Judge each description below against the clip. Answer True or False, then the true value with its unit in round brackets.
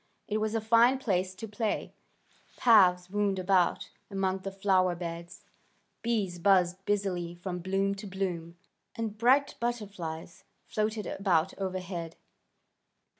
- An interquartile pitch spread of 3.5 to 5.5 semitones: False (2.9 semitones)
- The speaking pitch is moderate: False (195 Hz)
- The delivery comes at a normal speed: False (125 wpm)